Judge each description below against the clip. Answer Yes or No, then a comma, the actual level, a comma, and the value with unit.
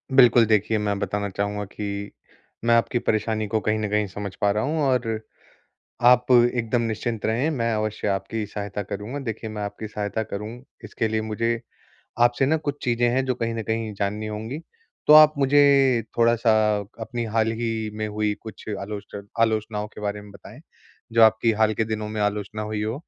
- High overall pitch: No, low, 110 Hz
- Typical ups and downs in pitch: No, narrow, 2.0 semitones